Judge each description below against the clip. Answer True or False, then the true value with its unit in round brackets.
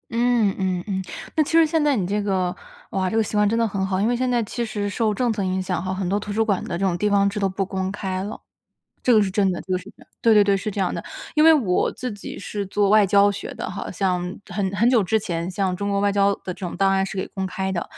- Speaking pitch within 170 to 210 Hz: True (200 Hz)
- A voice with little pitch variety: True (2.3 semitones)